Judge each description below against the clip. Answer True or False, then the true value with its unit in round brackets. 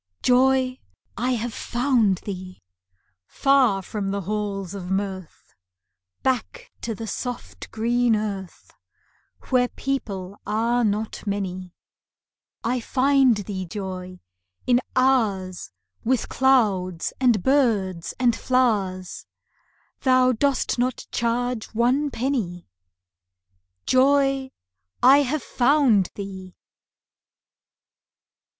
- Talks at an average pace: False (95 wpm)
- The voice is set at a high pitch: True (230 Hz)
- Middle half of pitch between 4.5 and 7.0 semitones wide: True (4.8 semitones)